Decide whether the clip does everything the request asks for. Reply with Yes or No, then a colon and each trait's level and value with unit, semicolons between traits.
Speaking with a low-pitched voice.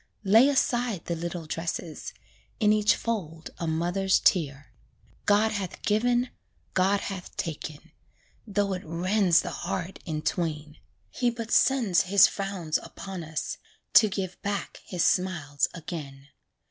No: medium, 185 Hz